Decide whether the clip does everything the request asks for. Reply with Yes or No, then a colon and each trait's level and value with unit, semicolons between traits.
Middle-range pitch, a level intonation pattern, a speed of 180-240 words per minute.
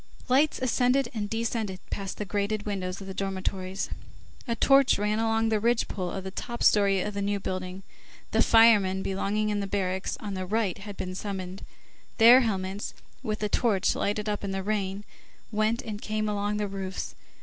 No: high, 205 Hz; narrow, 2.3 semitones; average, 185 wpm